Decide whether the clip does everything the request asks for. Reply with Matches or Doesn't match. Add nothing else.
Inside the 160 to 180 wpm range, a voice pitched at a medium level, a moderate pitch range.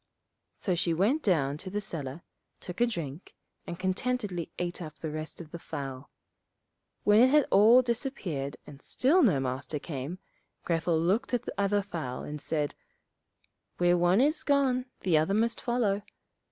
Doesn't match